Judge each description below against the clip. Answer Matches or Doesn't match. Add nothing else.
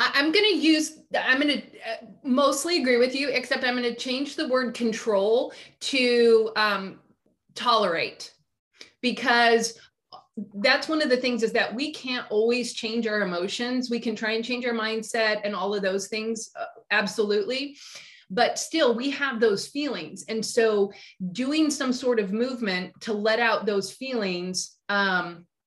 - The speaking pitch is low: Doesn't match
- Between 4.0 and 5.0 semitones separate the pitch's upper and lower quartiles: Doesn't match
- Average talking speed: Matches